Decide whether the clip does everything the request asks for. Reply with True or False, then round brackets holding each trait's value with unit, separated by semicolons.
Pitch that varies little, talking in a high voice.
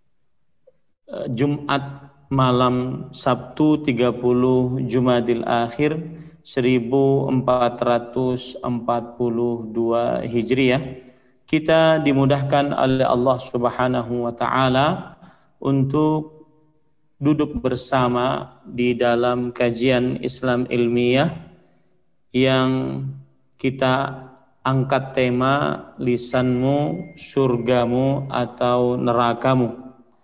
False (2.0 semitones; 130 Hz)